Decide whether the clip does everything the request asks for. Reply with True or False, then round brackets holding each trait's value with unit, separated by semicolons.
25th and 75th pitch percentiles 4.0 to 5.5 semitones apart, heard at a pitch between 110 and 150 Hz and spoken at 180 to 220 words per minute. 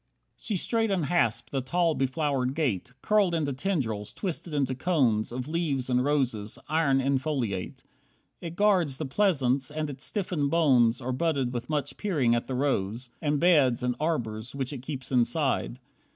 False (4.4 semitones; 140 Hz; 165 wpm)